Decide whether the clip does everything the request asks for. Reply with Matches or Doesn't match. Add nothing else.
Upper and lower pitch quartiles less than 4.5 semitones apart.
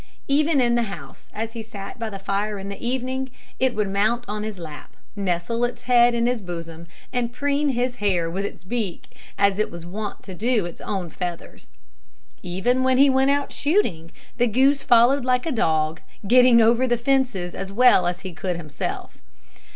Doesn't match